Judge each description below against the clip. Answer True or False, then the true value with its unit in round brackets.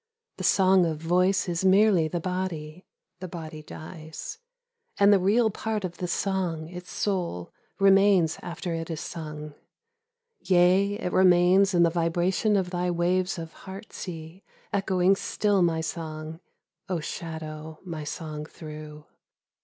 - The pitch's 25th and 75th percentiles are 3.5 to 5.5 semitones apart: False (2.9 semitones)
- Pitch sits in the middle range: True (175 Hz)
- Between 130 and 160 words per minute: True (140 wpm)